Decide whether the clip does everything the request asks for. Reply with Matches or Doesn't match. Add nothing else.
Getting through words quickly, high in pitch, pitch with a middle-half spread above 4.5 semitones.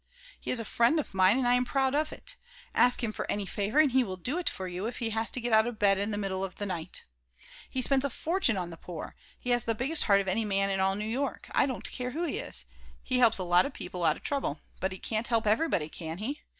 Matches